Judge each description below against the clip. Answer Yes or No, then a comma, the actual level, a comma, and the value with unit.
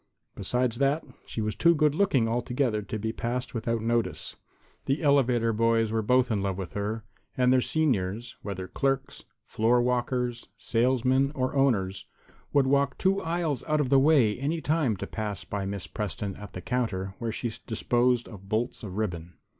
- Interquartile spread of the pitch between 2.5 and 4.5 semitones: Yes, average, 4.0 semitones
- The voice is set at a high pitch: No, low, 120 Hz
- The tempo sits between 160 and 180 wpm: Yes, average, 175 wpm